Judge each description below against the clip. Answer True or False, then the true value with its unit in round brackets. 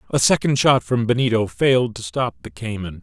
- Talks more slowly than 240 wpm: True (200 wpm)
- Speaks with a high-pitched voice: False (115 Hz)